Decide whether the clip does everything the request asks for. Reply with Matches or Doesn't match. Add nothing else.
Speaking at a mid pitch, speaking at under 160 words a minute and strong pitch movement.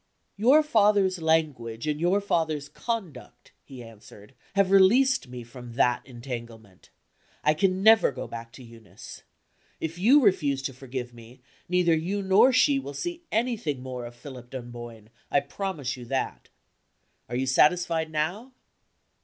Matches